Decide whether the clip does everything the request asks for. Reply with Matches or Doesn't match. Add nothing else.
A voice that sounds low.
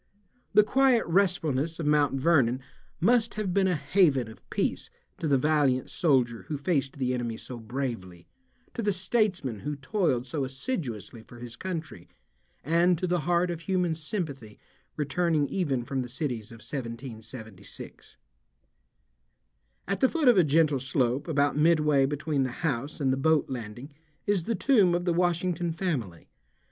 Doesn't match